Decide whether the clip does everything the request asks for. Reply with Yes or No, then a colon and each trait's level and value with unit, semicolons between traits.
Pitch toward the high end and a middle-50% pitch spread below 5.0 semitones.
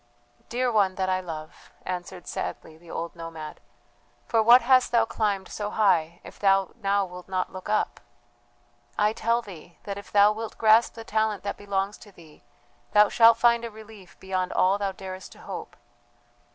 Yes: high, 200 Hz; average, 2.9 semitones